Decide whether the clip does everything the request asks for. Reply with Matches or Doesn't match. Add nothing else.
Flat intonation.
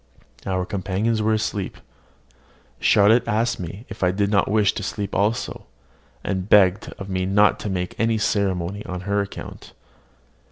Matches